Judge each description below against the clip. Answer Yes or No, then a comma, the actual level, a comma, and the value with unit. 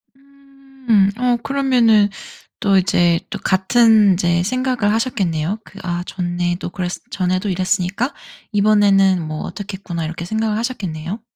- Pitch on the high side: Yes, high, 200 Hz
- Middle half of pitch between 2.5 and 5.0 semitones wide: Yes, average, 4.7 semitones